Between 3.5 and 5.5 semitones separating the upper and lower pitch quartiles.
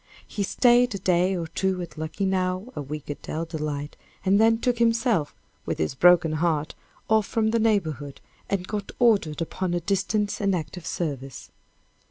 Yes: average, 5.1 semitones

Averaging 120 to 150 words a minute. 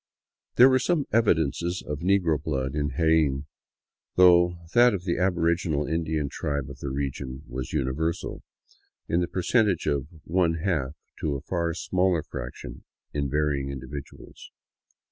Yes: average, 145 wpm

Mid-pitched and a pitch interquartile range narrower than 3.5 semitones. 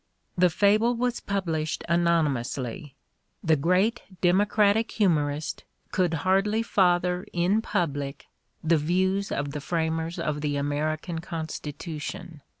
No: medium, 170 Hz; average, 4.0 semitones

